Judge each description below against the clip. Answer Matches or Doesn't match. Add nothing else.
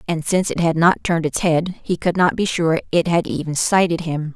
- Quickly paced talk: Matches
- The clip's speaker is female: Matches